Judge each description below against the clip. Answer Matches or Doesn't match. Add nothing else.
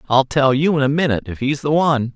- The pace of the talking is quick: Matches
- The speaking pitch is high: Doesn't match